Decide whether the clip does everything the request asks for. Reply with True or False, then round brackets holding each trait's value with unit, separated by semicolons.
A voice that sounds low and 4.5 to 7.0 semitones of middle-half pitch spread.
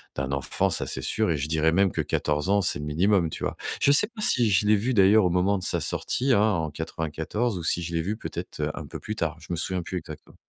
True (90 Hz; 4.8 semitones)